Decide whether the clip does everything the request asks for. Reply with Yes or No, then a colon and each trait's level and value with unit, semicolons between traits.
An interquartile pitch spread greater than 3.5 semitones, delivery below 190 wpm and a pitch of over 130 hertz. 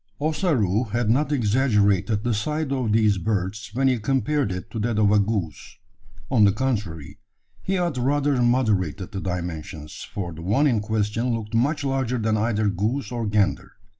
No: average, 4.4 semitones; average, 170 wpm; low, 110 Hz